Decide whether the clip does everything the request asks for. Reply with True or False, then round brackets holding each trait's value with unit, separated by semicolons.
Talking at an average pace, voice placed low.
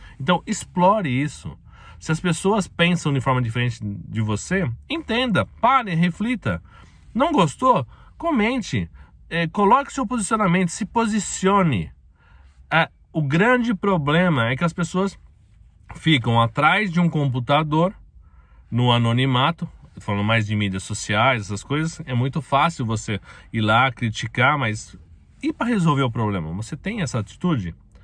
False (135 wpm; 145 Hz)